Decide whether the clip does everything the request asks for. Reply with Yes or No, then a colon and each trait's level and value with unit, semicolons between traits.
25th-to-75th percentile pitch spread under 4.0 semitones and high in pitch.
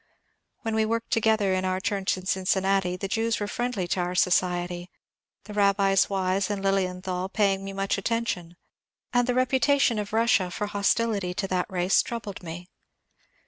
Yes: average, 3.1 semitones; high, 195 Hz